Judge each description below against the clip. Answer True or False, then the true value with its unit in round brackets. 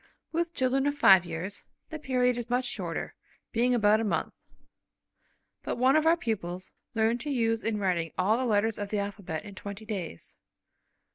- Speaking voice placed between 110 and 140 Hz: False (220 Hz)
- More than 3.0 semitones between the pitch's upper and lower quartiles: True (4.0 semitones)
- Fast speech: False (180 wpm)